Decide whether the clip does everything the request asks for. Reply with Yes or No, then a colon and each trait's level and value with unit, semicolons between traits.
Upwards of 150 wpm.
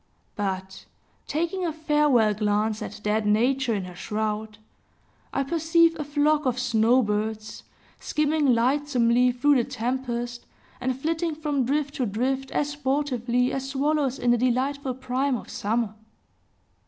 No: average, 140 wpm